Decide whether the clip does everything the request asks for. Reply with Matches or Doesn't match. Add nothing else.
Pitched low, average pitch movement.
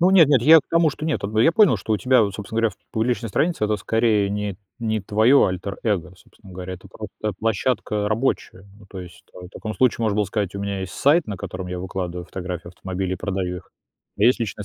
Matches